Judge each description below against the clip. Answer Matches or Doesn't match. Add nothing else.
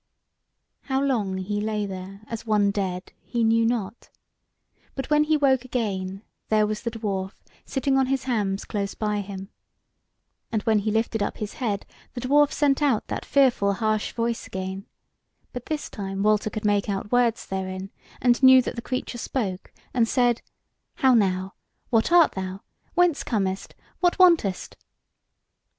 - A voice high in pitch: Matches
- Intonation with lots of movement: Doesn't match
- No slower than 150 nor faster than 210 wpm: Matches